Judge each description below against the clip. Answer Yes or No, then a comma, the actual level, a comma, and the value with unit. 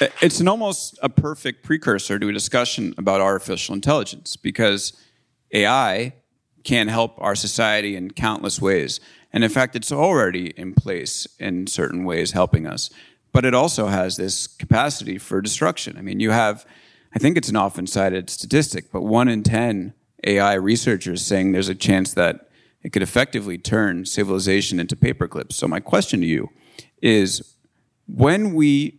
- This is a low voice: Yes, low, 105 Hz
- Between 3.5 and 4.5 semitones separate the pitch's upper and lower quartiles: No, average, 4.9 semitones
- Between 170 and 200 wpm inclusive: No, average, 160 wpm